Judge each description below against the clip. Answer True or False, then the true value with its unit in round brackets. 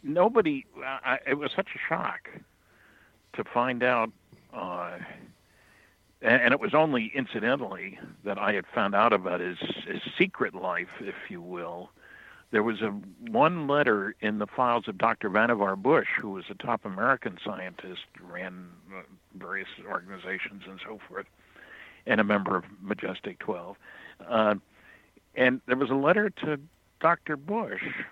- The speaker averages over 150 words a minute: False (145 wpm)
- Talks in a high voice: False (120 Hz)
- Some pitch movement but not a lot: False (5.7 semitones)